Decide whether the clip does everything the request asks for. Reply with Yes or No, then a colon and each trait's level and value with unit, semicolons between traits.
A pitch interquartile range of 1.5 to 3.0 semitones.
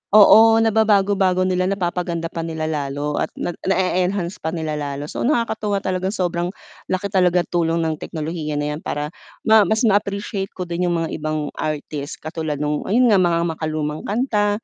No: average, 4.2 semitones